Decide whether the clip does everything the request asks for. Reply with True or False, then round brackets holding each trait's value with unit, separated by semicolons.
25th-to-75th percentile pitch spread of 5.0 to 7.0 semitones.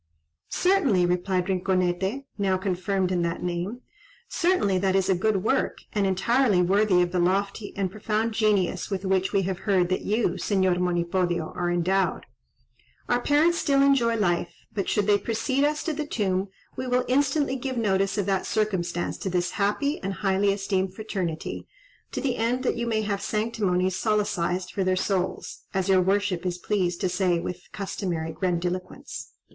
False (3.1 semitones)